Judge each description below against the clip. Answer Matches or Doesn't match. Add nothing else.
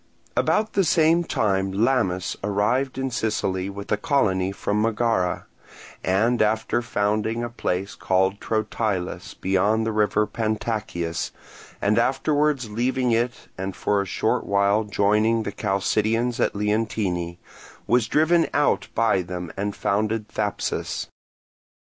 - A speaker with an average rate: Doesn't match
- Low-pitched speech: Matches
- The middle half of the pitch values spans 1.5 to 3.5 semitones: Matches